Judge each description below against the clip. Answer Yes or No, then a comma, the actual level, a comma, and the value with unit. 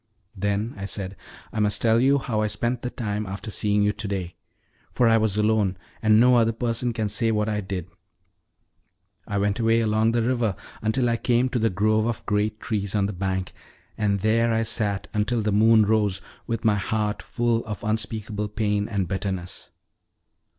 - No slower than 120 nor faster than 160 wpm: No, average, 190 wpm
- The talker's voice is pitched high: No, low, 110 Hz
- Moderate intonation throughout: No, narrow, 1.9 semitones